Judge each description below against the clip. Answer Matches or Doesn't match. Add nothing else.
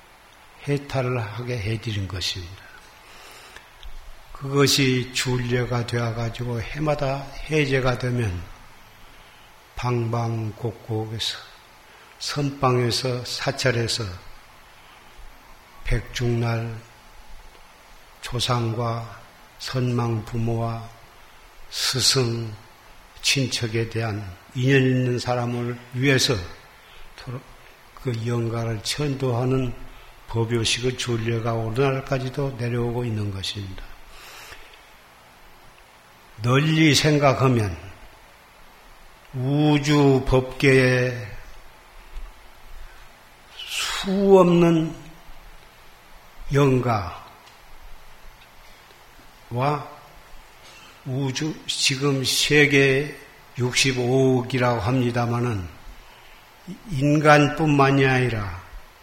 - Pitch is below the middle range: Matches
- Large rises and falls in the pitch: Doesn't match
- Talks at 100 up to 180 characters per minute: Matches